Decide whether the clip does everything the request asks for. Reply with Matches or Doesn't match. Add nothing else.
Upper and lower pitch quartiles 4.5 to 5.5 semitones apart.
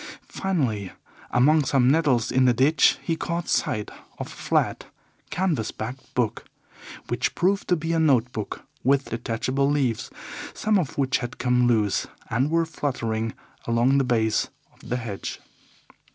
Matches